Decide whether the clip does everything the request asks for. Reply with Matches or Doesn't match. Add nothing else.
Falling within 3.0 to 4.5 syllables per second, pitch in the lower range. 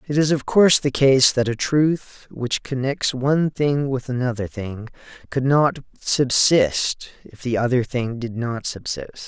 Matches